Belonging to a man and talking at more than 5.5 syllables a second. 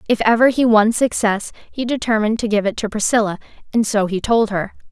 No: female; 5.7 syllables/s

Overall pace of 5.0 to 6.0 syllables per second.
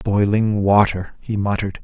No: 4.8 syllables/s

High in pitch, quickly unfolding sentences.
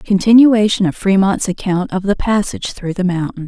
No: high, 195 Hz; average, 175 wpm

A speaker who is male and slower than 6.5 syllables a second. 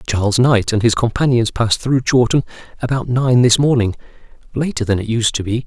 Yes: male; 5.7 syllables/s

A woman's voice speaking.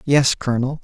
No: male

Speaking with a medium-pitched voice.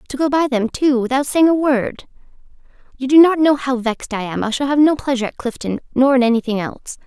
No: very high, 260 Hz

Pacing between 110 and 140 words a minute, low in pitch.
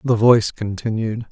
Yes: slow, 135 wpm; low, 110 Hz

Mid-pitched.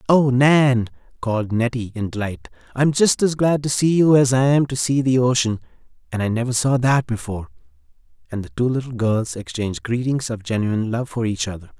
No: low, 120 Hz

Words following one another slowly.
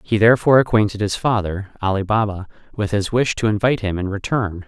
No: average, 195 wpm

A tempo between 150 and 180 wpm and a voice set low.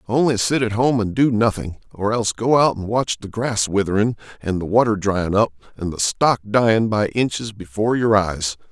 No: fast, 205 wpm; low, 110 Hz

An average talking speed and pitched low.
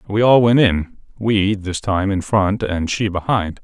Yes: average, 180 wpm; low, 100 Hz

